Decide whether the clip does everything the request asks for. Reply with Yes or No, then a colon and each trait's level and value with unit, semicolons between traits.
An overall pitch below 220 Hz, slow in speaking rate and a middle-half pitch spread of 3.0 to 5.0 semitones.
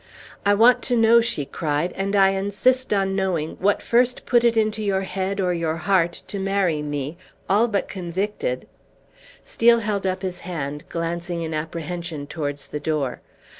No: high, 190 Hz; average, 170 wpm; average, 4.1 semitones